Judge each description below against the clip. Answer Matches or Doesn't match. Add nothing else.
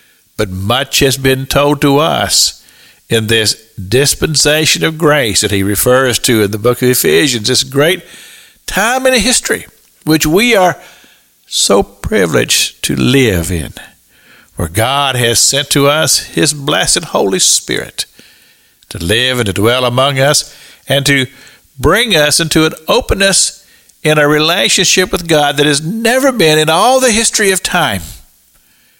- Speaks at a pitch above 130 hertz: Matches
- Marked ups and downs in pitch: Doesn't match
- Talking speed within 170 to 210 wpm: Doesn't match